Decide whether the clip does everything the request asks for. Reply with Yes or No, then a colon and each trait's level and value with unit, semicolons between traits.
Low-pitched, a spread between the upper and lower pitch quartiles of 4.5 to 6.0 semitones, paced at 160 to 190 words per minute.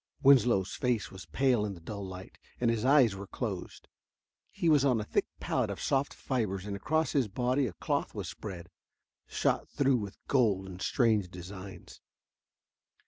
Yes: low, 110 Hz; average, 5.3 semitones; average, 170 wpm